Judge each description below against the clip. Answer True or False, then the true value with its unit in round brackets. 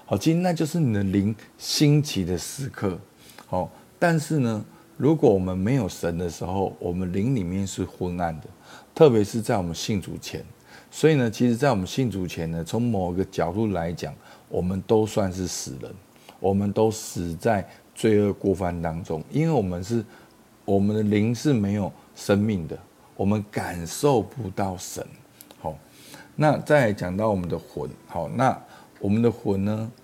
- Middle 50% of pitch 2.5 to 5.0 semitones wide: True (4.3 semitones)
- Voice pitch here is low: True (105 Hz)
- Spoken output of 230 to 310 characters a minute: True (245 characters per minute)